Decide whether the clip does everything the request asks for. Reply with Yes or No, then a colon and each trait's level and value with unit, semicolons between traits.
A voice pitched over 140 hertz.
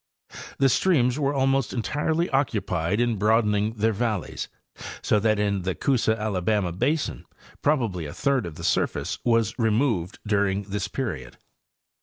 No: low, 110 Hz